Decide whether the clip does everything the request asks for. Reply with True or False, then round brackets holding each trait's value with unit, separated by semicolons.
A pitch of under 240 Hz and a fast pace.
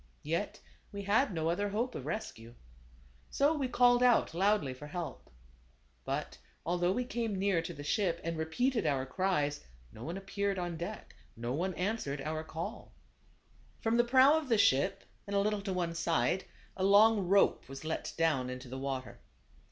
False (185 Hz; 175 wpm)